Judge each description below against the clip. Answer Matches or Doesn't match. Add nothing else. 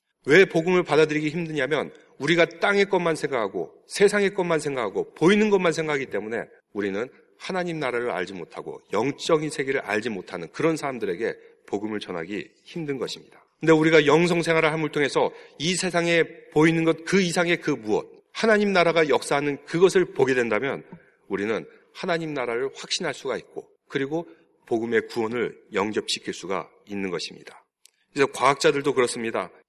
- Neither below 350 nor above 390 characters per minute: Matches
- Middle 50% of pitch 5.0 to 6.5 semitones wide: Matches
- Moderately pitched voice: Matches